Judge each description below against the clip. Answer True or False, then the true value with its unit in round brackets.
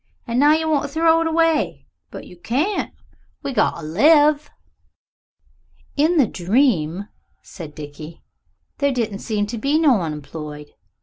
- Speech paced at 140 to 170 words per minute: True (145 wpm)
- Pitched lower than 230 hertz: False (245 Hz)